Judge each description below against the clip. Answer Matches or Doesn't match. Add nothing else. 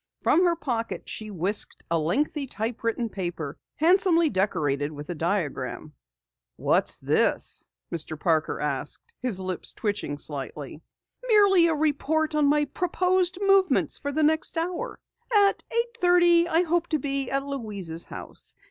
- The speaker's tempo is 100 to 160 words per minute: Matches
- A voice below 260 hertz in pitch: Doesn't match